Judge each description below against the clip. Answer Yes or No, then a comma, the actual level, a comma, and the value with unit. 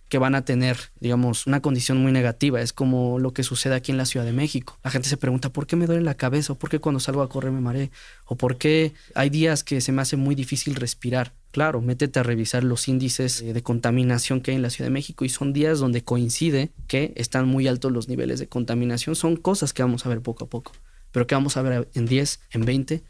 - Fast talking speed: Yes, fast, 250 wpm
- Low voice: Yes, low, 130 Hz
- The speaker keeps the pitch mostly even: Yes, narrow, 2.2 semitones